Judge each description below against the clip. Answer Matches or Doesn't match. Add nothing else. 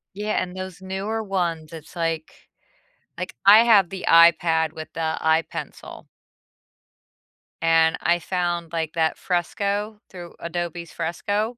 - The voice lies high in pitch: Doesn't match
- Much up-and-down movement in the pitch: Doesn't match